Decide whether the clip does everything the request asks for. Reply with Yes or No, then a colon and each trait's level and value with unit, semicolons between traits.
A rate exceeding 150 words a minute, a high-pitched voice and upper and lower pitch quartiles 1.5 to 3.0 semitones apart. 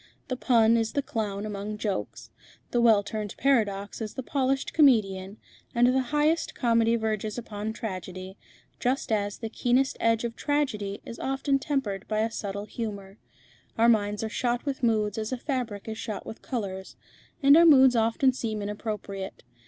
No: average, 170 wpm; high, 225 Hz; average, 3.6 semitones